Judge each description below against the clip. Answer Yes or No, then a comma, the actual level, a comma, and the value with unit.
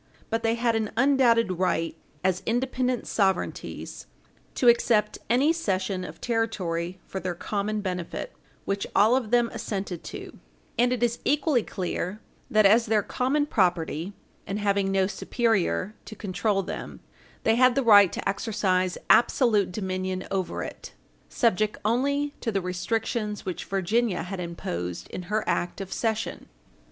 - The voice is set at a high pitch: Yes, high, 210 Hz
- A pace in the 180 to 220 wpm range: No, average, 145 wpm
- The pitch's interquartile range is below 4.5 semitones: Yes, average, 4.0 semitones